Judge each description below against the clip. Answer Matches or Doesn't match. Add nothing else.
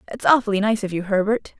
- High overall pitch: Matches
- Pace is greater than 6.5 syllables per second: Matches